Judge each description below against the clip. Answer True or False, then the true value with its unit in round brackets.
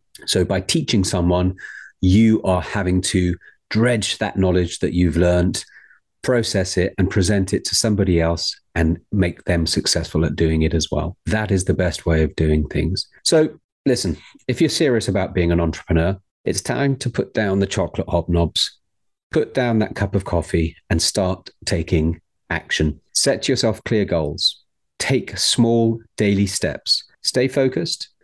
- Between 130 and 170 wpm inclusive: True (160 wpm)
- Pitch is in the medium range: False (95 Hz)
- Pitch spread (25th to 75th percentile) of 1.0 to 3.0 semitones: False (4.2 semitones)